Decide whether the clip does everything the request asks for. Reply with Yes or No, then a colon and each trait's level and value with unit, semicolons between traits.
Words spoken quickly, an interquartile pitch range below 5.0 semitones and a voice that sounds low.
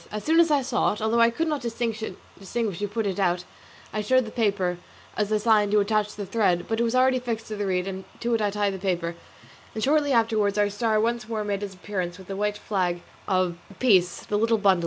No: fast, 240 wpm; average, 2.9 semitones; high, 210 Hz